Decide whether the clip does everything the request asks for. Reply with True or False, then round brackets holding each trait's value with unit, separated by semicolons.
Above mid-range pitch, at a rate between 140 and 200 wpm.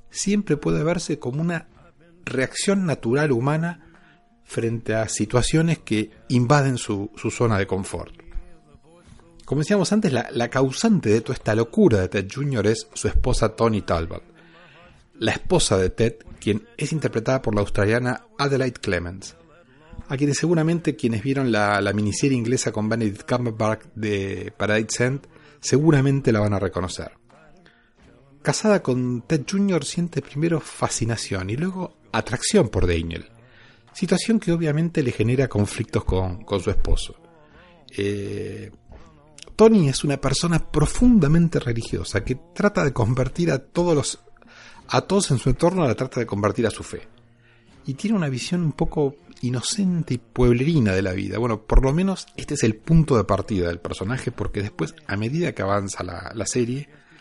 False (125 Hz; 155 wpm)